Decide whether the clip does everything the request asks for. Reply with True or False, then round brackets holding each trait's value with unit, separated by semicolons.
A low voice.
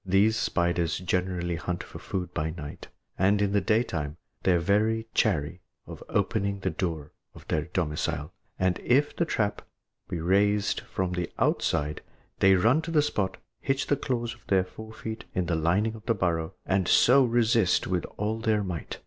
True (95 Hz)